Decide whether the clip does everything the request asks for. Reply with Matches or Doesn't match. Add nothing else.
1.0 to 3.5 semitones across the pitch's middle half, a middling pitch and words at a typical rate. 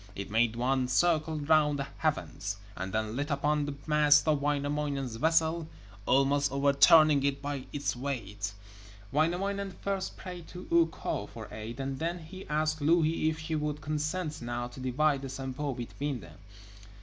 Matches